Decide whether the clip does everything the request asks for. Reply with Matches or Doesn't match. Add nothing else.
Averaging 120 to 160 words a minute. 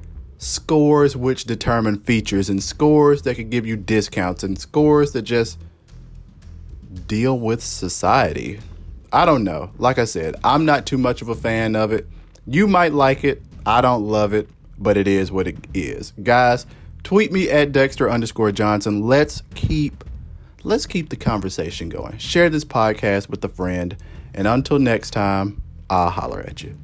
Doesn't match